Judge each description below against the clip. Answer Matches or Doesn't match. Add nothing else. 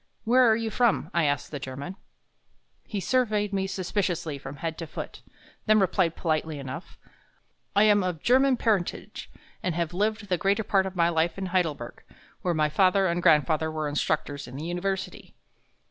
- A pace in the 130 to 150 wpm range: Doesn't match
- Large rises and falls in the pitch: Doesn't match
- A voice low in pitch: Doesn't match